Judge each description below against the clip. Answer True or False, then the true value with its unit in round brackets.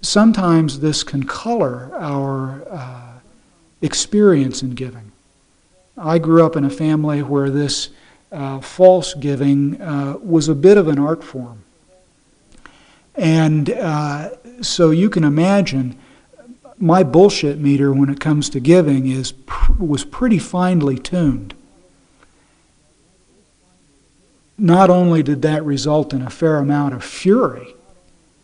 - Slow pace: True (125 wpm)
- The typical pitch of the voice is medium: True (150 Hz)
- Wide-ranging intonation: False (3.8 semitones)